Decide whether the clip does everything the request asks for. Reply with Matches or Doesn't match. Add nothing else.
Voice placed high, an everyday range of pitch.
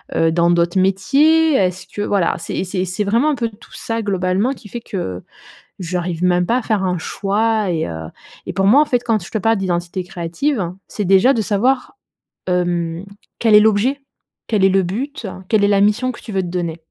Matches